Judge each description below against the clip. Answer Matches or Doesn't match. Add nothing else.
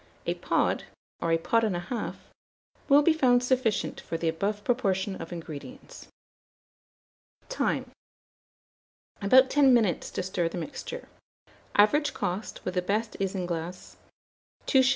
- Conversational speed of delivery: Doesn't match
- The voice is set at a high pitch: Matches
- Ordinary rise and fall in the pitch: Doesn't match